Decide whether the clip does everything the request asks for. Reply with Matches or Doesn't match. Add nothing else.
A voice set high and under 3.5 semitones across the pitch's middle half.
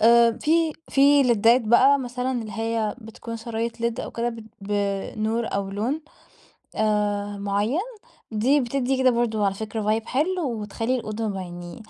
Matches